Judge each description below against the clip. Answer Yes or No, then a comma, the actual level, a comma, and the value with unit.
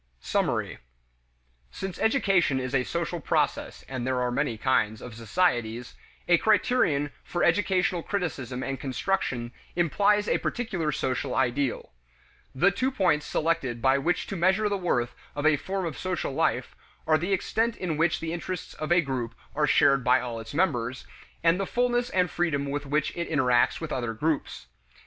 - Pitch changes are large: Yes, wide, 6.1 semitones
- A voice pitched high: No, medium, 155 Hz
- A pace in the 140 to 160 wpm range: No, average, 170 wpm